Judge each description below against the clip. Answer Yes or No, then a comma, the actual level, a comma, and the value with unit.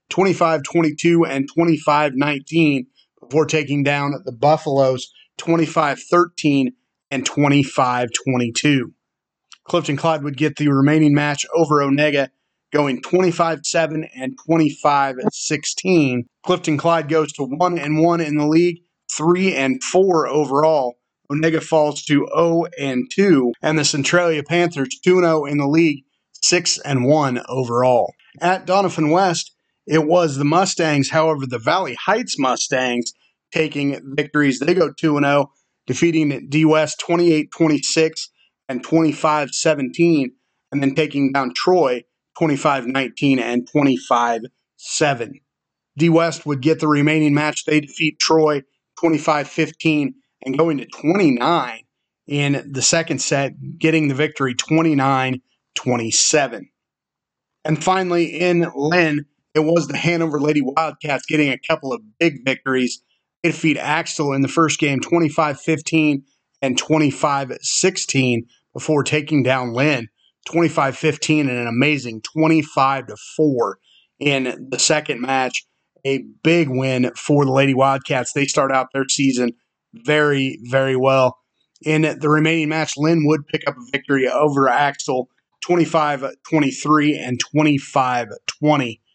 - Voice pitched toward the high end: No, medium, 150 Hz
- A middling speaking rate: No, slow, 130 wpm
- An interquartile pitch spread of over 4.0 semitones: No, average, 2.9 semitones